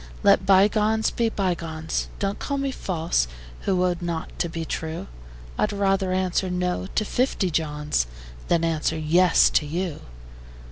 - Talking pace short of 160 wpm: Yes, average, 145 wpm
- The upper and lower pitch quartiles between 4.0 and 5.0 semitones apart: No, average, 3.3 semitones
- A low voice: No, medium, 180 Hz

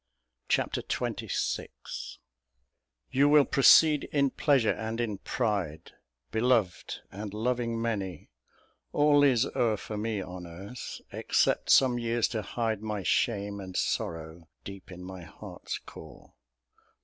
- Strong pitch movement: No, average, 4.4 semitones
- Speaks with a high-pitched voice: No, low, 110 Hz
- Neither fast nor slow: No, slow, 125 wpm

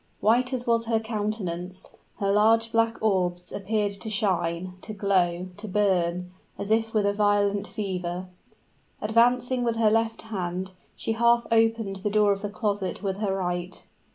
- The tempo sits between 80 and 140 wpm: No, average, 160 wpm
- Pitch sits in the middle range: No, high, 205 Hz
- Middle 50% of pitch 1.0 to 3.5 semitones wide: Yes, average, 3.1 semitones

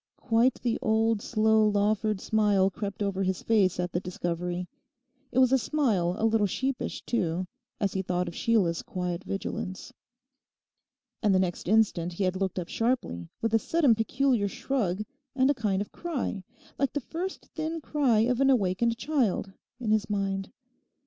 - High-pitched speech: Yes, high, 215 Hz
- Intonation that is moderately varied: Yes, average, 4.2 semitones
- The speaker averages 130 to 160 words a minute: No, average, 170 wpm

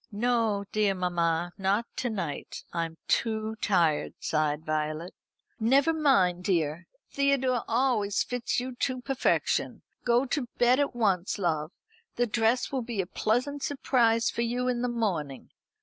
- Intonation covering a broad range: Yes, wide, 5.8 semitones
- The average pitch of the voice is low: No, high, 220 Hz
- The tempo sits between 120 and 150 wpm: Yes, average, 145 wpm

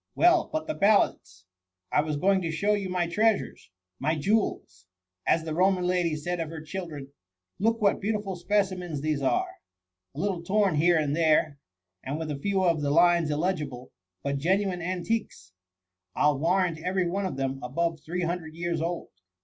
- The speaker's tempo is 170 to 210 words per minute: Yes, average, 175 wpm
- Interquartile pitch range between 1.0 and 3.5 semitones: No, average, 3.9 semitones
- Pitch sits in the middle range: Yes, medium, 170 Hz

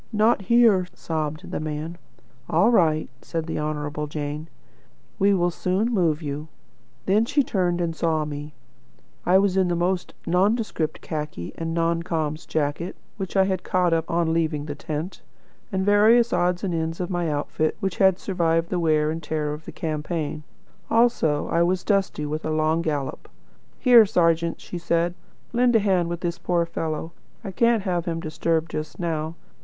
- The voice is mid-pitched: Yes, medium, 170 Hz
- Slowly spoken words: No, average, 175 wpm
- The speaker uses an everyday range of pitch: Yes, average, 3.3 semitones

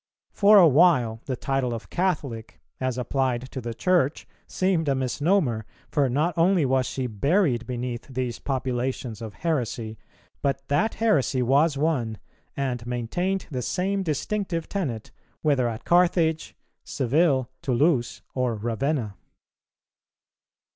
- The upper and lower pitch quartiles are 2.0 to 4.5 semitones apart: No, average, 5.3 semitones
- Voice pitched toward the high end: No, low, 135 Hz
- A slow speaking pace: Yes, slow, 125 wpm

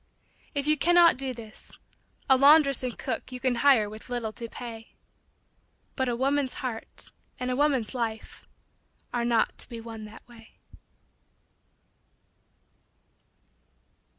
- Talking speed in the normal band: No, slow, 130 wpm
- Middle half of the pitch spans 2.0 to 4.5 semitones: Yes, average, 3.2 semitones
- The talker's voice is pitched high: Yes, high, 245 Hz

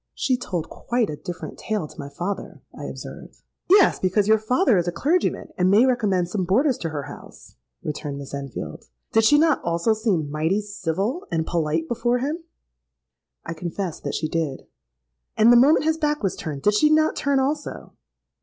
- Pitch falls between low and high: No, high, 195 Hz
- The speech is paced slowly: No, average, 175 wpm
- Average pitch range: No, wide, 8.0 semitones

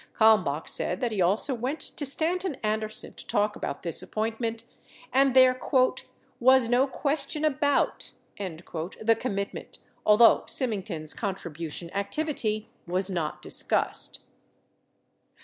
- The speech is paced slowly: Yes, slow, 115 wpm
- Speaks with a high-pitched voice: Yes, high, 220 Hz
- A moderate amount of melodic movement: No, wide, 5.7 semitones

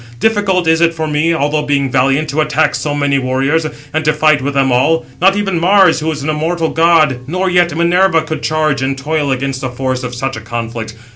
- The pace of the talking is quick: Yes, fast, 220 wpm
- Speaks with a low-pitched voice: No, medium, 155 Hz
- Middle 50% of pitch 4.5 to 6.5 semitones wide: No, average, 3.3 semitones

